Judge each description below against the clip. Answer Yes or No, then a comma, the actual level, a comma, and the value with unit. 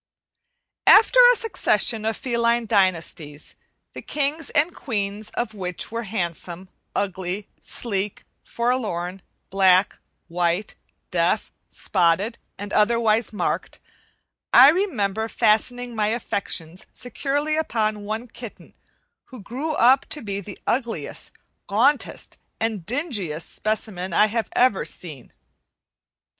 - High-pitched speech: Yes, high, 215 Hz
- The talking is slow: Yes, slow, 110 wpm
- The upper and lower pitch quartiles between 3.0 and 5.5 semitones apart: Yes, average, 4.4 semitones